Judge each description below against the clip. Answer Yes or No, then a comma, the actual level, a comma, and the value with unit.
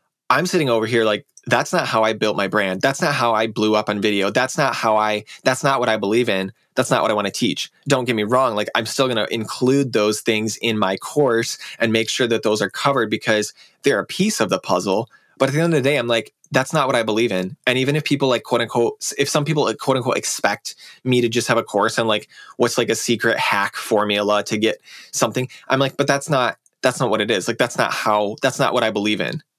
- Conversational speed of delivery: No, fast, 270 wpm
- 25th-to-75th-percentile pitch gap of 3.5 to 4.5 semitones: Yes, average, 3.9 semitones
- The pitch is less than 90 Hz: No, low, 115 Hz